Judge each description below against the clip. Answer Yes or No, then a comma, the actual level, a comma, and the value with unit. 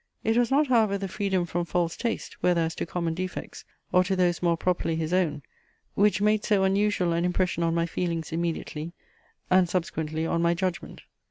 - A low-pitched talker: No, medium, 180 Hz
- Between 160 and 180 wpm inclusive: No, average, 190 wpm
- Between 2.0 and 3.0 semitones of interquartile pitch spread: Yes, narrow, 2.5 semitones